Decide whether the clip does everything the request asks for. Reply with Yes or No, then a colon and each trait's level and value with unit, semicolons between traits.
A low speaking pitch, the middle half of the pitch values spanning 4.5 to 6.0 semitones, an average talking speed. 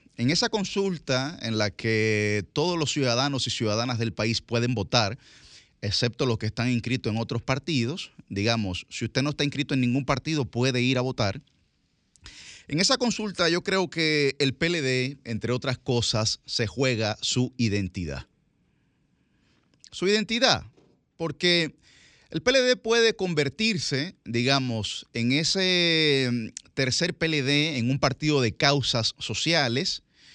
Yes: low, 130 Hz; average, 5.1 semitones; average, 135 wpm